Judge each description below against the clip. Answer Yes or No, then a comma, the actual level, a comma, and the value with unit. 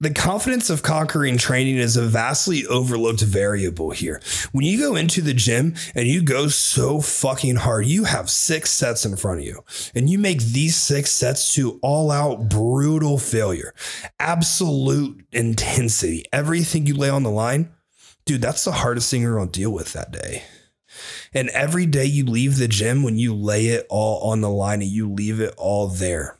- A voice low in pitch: Yes, low, 130 Hz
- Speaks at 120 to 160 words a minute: No, average, 190 wpm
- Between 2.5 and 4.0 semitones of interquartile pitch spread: No, average, 5.1 semitones